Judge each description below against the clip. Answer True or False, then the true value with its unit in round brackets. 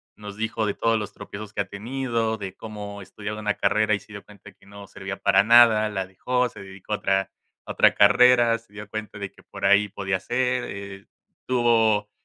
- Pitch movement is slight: True (2.1 semitones)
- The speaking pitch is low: True (105 Hz)